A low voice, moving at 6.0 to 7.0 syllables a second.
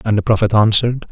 Yes: low, 110 Hz; 6.9 syllables/s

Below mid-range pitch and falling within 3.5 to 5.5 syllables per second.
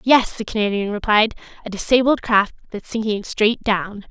No: high, 215 Hz; 4.9 syllables/s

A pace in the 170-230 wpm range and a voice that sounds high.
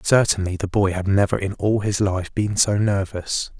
No: average, 200 wpm; low, 100 Hz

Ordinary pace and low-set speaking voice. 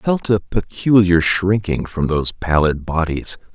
Yes: average, 150 wpm; very low, 90 Hz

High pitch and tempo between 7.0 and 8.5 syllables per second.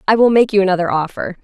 Yes: high, 200 Hz; 7.1 syllables/s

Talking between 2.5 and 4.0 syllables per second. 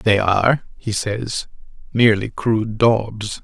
Yes: 3.9 syllables/s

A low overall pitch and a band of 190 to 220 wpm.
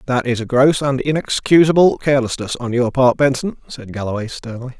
No: low, 130 Hz; average, 165 wpm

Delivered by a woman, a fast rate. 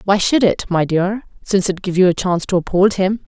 Yes: female; fast, 250 wpm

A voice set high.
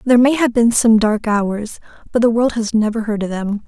Yes: high, 225 Hz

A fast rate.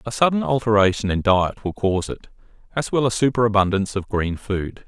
No: average, 185 wpm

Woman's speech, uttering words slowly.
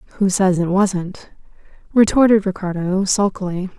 Yes: female; slow, 110 wpm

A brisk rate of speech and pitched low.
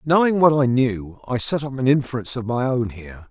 Yes: fast, 235 wpm; low, 125 Hz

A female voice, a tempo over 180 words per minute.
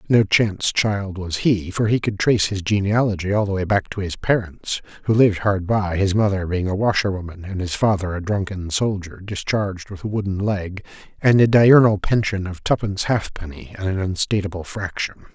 No: male; average, 190 wpm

